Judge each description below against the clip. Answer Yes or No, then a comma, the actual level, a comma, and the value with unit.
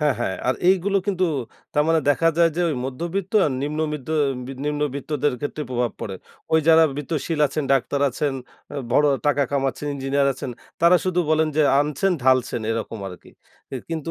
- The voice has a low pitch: No, medium, 150 Hz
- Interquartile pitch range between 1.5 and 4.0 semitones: Yes, average, 3.3 semitones